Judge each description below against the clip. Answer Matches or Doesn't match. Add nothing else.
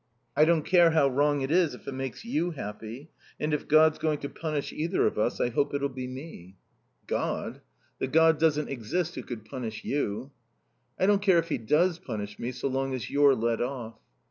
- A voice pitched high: Doesn't match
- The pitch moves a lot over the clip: Doesn't match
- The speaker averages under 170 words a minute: Doesn't match